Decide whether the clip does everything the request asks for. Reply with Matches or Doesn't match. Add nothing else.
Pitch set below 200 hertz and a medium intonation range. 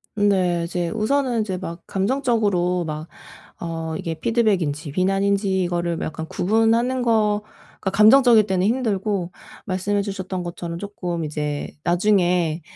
Matches